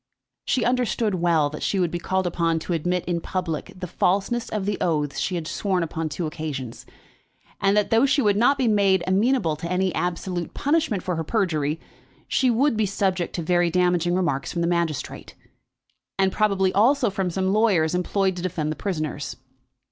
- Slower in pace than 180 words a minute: No, average, 185 wpm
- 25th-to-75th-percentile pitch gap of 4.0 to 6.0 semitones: No, average, 3.5 semitones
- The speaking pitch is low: No, medium, 180 Hz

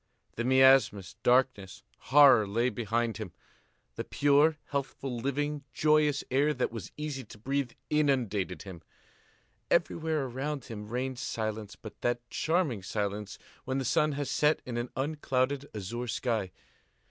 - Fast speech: No, slow, 135 wpm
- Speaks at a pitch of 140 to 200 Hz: No, low, 130 Hz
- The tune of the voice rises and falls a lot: No, average, 4.4 semitones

